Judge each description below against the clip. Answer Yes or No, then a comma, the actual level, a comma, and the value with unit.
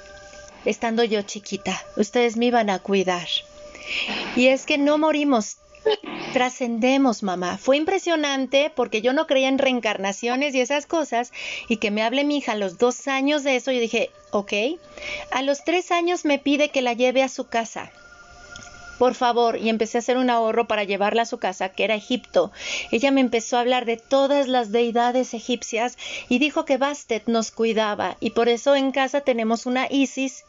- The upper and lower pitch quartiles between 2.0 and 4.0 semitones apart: Yes, average, 3.6 semitones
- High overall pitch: Yes, very high, 250 Hz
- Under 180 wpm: No, average, 185 wpm